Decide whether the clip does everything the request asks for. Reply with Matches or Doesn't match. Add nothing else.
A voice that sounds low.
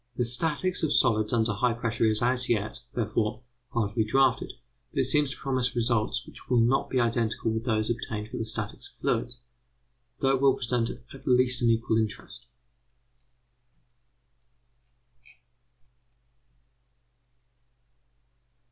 Matches